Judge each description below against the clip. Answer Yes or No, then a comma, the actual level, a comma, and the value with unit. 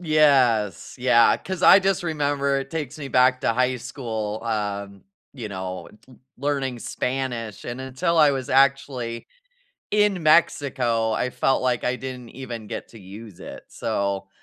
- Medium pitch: No, low, 125 Hz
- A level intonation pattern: No, average, 3.8 semitones